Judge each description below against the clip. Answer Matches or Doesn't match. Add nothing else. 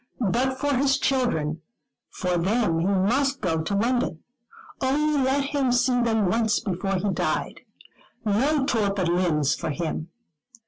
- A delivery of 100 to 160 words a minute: Matches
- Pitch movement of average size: Doesn't match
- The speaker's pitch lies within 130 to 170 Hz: Doesn't match